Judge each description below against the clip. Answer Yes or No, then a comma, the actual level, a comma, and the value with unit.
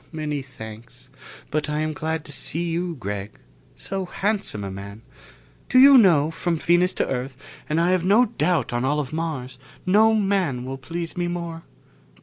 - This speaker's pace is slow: No, average, 175 wpm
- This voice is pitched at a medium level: Yes, medium, 160 Hz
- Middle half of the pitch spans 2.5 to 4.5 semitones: No, average, 5.3 semitones